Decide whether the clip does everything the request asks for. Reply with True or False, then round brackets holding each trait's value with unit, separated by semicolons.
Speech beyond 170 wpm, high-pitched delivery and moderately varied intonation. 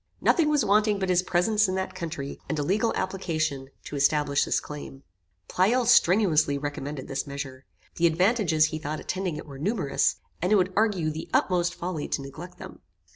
False (180 wpm; 170 Hz; 4.7 semitones)